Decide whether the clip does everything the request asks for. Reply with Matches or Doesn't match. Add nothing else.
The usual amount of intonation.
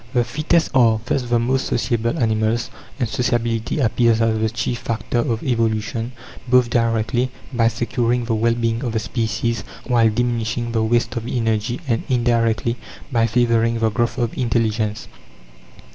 Doesn't match